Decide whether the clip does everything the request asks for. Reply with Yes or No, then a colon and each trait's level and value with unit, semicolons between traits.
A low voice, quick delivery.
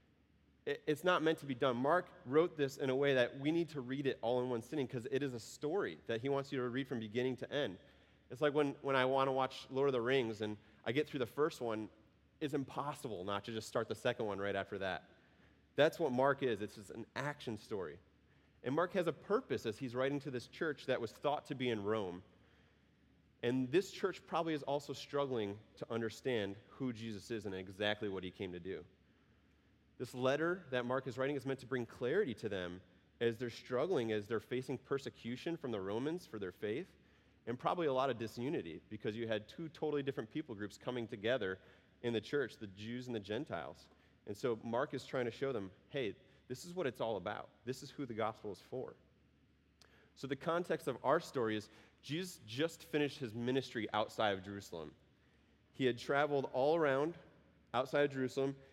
Yes: low, 125 Hz; fast, 215 wpm